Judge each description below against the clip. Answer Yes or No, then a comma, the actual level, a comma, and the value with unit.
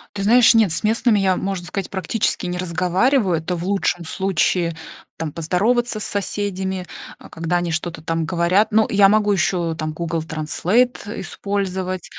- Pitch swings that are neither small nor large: Yes, average, 3.3 semitones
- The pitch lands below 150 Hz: No, medium, 185 Hz